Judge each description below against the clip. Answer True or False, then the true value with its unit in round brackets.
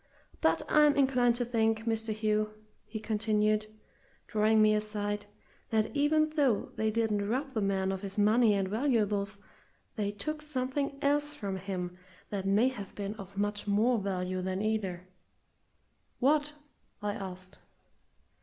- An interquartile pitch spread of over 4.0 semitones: False (3.4 semitones)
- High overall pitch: True (215 Hz)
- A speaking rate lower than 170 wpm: True (145 wpm)